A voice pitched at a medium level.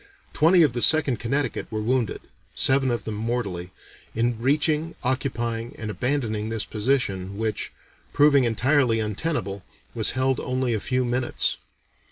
No: low, 120 Hz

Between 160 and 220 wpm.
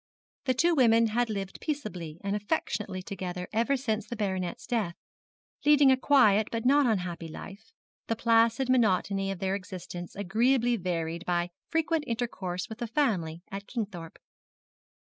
No: average, 145 wpm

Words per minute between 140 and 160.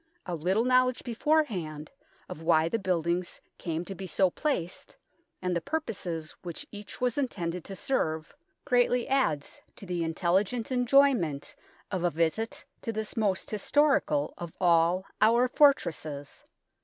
Yes: average, 145 wpm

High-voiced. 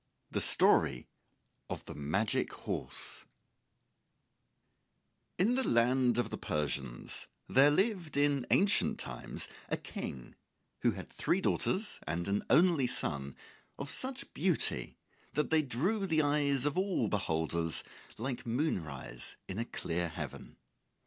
No: low, 130 Hz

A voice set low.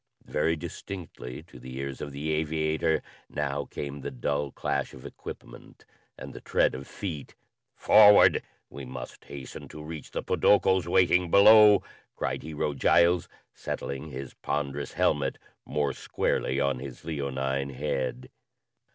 Yes: very low, 70 Hz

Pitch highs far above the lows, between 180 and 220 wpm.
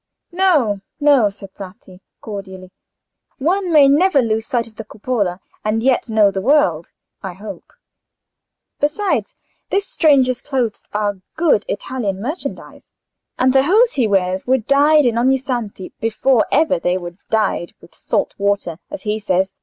No: wide, 6.0 semitones; average, 145 wpm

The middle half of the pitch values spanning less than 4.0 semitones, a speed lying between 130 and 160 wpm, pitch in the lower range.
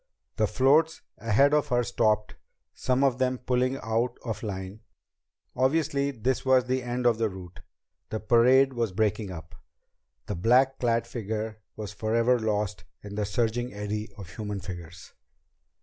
Yes: average, 3.4 semitones; average, 150 wpm; low, 115 Hz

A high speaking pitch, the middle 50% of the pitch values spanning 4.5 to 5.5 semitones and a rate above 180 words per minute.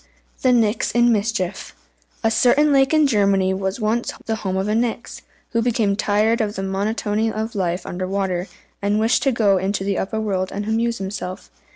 No: high, 210 Hz; average, 3.0 semitones; average, 190 wpm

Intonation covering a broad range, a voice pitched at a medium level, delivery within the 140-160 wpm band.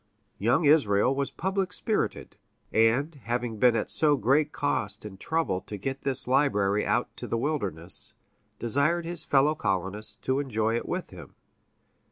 No: wide, 5.8 semitones; low, 125 Hz; average, 155 wpm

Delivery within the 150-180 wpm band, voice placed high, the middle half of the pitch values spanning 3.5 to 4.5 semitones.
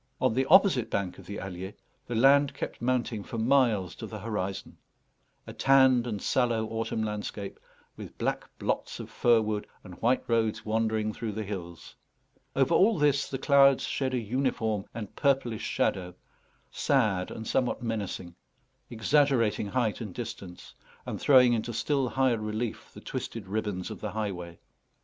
No: average, 160 wpm; low, 115 Hz; average, 3.8 semitones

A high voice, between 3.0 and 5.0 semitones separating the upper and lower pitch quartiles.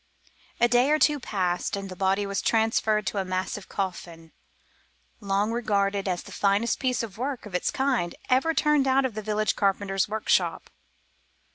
Yes: high, 210 Hz; average, 3.9 semitones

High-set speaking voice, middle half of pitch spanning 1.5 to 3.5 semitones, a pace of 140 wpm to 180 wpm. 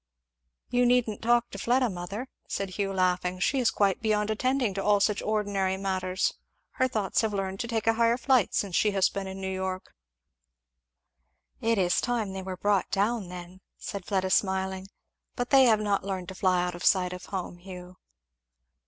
No: high, 195 Hz; average, 2.9 semitones; average, 190 wpm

